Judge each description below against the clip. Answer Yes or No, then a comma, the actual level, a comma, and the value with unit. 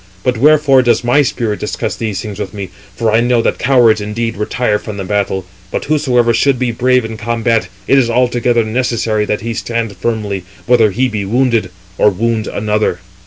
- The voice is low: Yes, low, 115 Hz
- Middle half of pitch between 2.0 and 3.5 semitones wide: Yes, average, 2.7 semitones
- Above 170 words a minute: Yes, average, 190 wpm